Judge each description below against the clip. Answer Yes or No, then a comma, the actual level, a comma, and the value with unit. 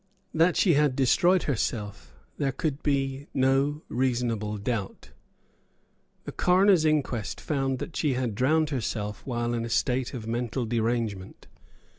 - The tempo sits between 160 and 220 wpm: No, slow, 135 wpm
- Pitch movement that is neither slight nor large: Yes, average, 4.1 semitones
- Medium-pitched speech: No, low, 130 Hz